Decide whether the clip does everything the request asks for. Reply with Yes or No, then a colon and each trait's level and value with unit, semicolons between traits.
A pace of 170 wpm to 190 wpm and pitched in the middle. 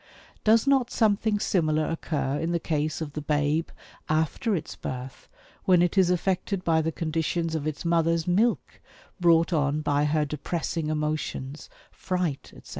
No: average, 155 wpm; medium, 160 Hz